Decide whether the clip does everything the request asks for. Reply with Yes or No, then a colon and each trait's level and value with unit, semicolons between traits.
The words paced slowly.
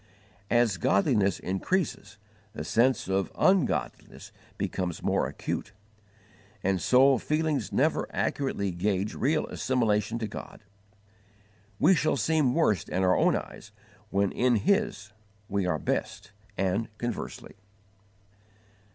Yes: slow, 115 wpm